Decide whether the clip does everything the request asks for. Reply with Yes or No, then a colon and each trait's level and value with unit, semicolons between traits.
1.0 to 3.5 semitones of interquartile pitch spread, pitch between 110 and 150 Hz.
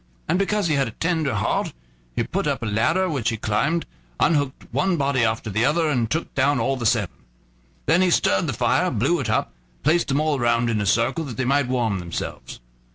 No: average, 5.3 semitones; low, 135 Hz